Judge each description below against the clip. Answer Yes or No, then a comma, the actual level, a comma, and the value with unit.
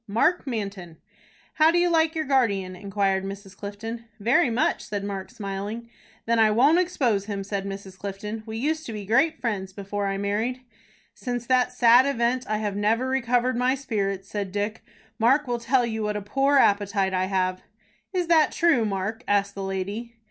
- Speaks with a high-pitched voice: Yes, high, 220 Hz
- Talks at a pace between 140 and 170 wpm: No, average, 185 wpm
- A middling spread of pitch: Yes, average, 4.1 semitones